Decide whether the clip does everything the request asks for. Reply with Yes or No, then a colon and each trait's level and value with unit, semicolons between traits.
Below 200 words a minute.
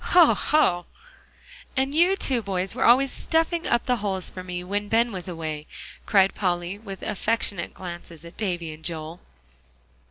Yes: average, 160 wpm